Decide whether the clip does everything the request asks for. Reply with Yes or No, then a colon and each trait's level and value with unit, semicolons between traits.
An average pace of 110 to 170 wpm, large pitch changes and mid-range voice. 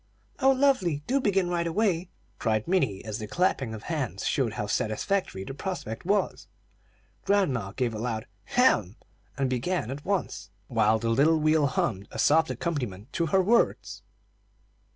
Yes: average, 155 wpm; wide, 8.7 semitones; medium, 145 Hz